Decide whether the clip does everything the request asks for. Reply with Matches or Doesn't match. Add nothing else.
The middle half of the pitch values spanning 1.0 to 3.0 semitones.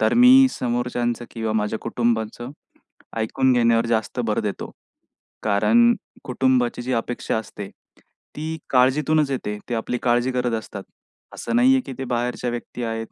Matches